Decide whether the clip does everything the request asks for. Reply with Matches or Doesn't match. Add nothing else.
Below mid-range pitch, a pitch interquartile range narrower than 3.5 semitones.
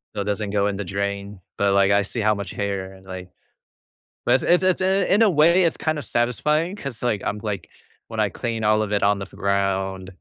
Doesn't match